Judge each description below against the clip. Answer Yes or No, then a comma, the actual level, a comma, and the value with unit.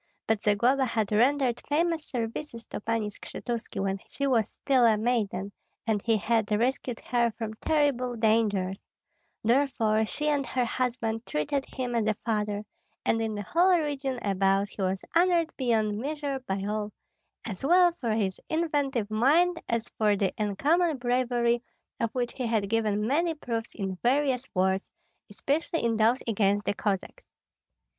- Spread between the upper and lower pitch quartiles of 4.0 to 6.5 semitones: Yes, average, 4.4 semitones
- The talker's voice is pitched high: Yes, high, 230 Hz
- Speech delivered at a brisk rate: No, average, 155 wpm